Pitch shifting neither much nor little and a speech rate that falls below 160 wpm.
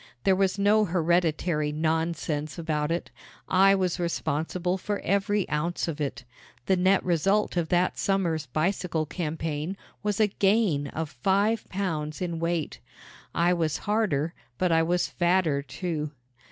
Yes: average, 3.5 semitones; average, 140 wpm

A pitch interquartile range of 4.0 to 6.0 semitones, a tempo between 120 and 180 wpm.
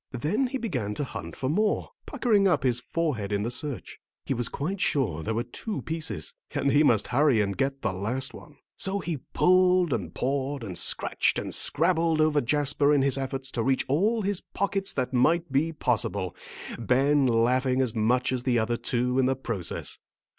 No: average, 4.9 semitones; average, 190 wpm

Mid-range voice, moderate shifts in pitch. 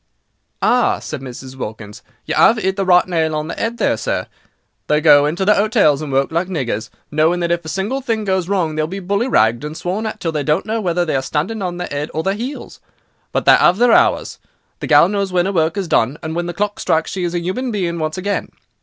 Yes: medium, 175 Hz; average, 4.4 semitones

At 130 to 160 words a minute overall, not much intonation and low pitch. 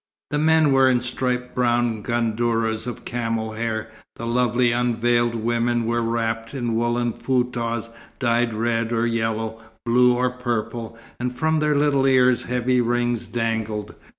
Yes: average, 145 wpm; narrow, 1.4 semitones; low, 120 Hz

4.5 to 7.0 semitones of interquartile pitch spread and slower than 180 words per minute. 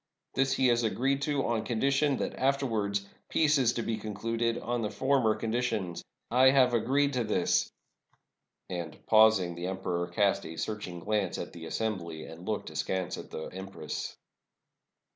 Yes: average, 5.2 semitones; average, 165 wpm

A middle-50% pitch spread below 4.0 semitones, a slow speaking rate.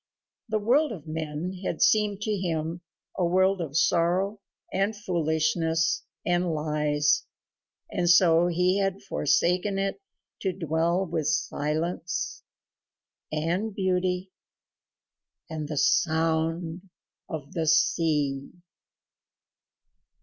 Yes: average, 3.0 semitones; slow, 100 wpm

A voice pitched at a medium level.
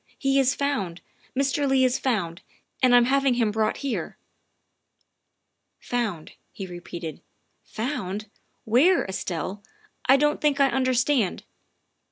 No: high, 245 Hz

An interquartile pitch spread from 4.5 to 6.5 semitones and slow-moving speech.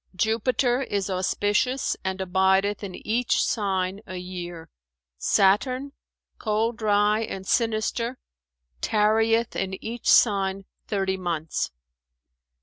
No: average, 3.0 semitones; slow, 100 wpm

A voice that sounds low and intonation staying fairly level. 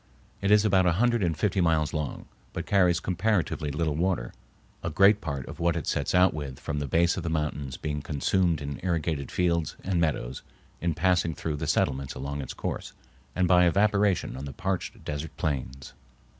No: very low, 85 Hz; average, 4.0 semitones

